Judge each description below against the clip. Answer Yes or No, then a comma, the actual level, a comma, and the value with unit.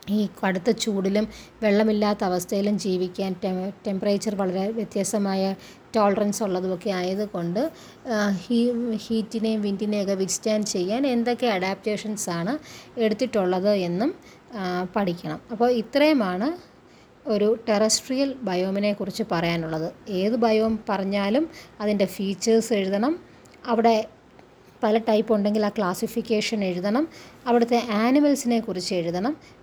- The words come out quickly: No, average, 95 wpm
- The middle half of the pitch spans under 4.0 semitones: Yes, average, 2.8 semitones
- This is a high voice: Yes, high, 210 Hz